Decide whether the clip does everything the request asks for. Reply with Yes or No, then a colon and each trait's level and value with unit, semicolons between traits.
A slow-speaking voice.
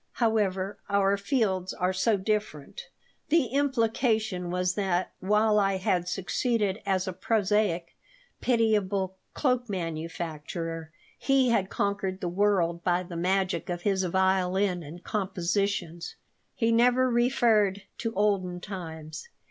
Yes: slow, 120 wpm